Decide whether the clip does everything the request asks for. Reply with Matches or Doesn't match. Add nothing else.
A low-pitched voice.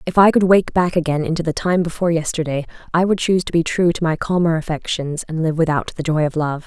Doesn't match